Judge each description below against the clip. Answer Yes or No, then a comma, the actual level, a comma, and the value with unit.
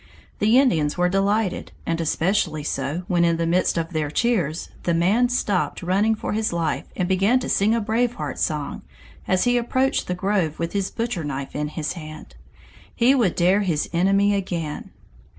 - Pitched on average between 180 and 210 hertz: Yes, medium, 185 Hz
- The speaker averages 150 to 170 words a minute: No, average, 185 wpm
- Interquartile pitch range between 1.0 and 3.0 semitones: No, average, 4.5 semitones